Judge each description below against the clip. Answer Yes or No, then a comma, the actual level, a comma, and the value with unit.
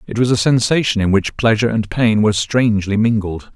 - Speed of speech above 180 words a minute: Yes, average, 200 wpm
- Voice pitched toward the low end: Yes, low, 110 Hz